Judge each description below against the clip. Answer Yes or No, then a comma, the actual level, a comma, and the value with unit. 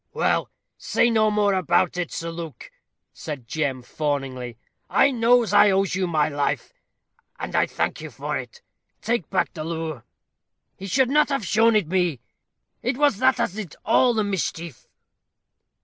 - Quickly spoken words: No, average, 165 wpm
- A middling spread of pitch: No, wide, 6.4 semitones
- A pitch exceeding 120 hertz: Yes, medium, 185 Hz